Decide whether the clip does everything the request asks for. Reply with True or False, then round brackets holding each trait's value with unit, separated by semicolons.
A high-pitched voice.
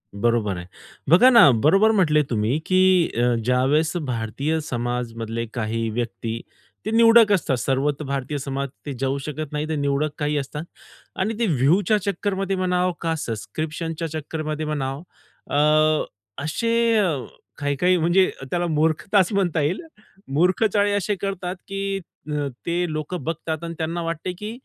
False (155 Hz)